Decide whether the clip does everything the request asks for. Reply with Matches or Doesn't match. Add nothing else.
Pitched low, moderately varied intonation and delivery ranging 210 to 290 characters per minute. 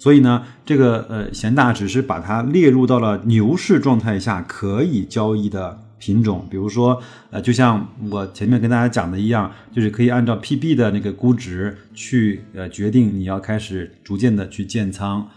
Matches